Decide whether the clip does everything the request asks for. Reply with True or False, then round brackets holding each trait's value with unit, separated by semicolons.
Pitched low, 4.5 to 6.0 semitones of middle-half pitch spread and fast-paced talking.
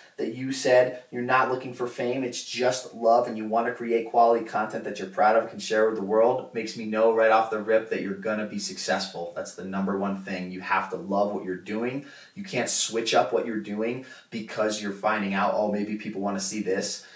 False (110 Hz; 3.1 semitones; 245 wpm)